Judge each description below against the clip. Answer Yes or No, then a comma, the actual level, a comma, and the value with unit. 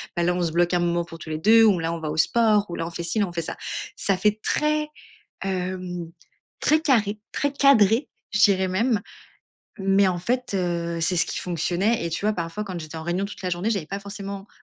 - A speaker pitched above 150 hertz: Yes, high, 190 Hz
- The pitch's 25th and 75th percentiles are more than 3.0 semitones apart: Yes, average, 3.5 semitones